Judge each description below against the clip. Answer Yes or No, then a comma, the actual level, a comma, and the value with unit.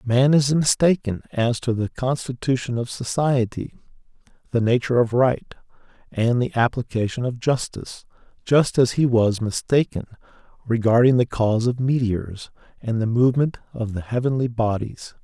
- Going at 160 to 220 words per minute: No, average, 140 wpm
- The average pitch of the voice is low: Yes, low, 120 Hz